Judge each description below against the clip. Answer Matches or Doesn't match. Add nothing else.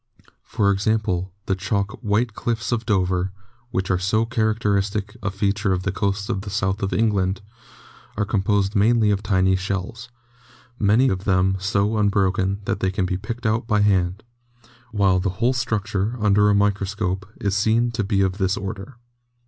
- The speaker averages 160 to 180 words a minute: Matches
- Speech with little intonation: Matches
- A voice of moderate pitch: Doesn't match